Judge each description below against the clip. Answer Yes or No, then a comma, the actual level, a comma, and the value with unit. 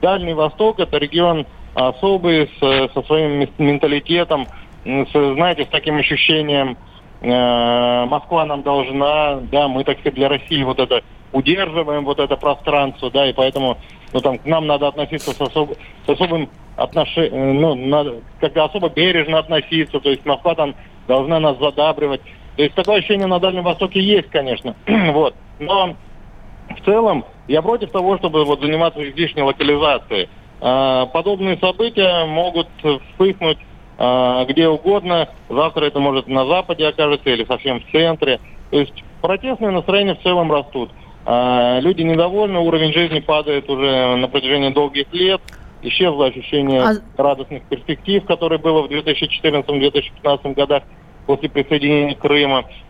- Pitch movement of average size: Yes, average, 3.4 semitones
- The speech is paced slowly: No, average, 140 wpm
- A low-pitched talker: No, medium, 150 Hz